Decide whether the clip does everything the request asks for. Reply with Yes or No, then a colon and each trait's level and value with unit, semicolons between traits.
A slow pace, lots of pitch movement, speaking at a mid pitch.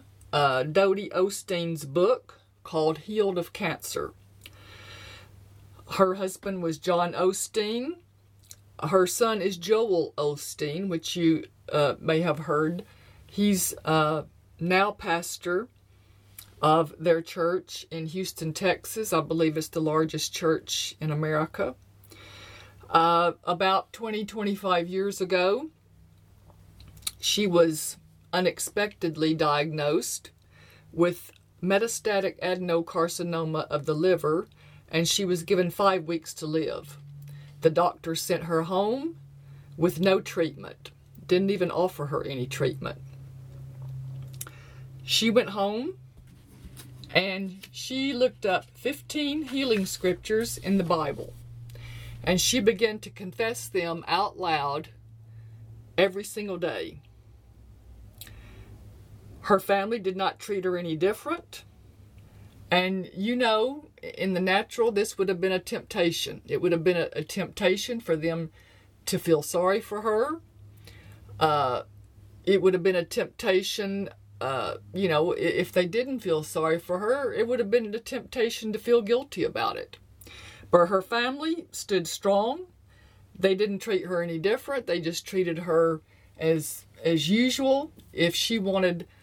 Yes: slow, 125 wpm; wide, 6.9 semitones; medium, 170 Hz